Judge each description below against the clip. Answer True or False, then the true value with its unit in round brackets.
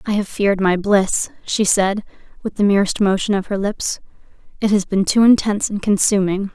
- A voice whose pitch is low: False (200 Hz)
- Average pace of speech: True (190 wpm)